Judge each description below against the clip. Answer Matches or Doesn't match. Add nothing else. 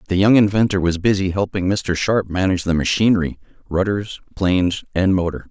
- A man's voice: Matches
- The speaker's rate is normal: Matches